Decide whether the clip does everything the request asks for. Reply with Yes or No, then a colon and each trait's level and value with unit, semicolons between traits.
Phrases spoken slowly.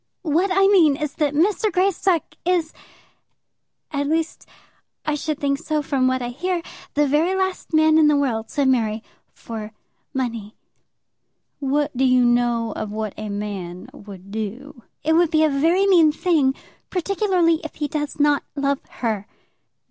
No: average, 160 wpm